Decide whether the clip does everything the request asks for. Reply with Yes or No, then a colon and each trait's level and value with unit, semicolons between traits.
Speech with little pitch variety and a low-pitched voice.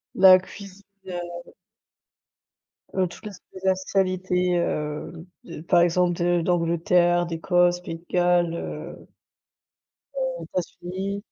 No: narrow, 1.5 semitones; medium, 180 Hz